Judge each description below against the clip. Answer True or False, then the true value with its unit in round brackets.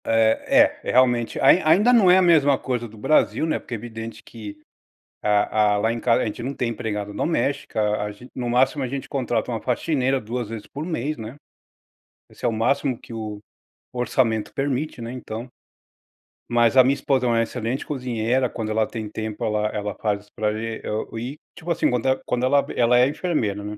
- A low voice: True (120 Hz)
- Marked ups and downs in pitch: False (3.5 semitones)